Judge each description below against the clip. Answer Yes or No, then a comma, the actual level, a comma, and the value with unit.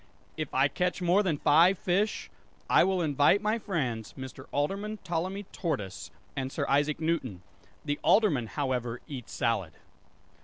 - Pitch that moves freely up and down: Yes, wide, 5.9 semitones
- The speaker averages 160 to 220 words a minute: No, average, 145 wpm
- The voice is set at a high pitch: No, medium, 150 Hz